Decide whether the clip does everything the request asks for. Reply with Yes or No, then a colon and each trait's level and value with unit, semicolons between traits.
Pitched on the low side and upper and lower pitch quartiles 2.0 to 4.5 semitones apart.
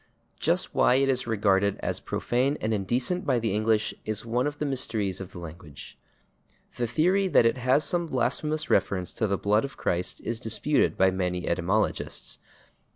No: low, 115 Hz; average, 5.3 semitones